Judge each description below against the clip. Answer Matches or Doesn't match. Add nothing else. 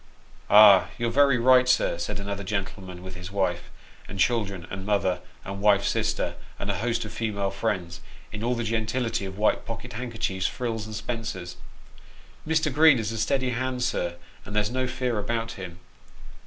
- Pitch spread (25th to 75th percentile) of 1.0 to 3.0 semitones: Doesn't match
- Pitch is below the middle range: Matches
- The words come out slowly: Doesn't match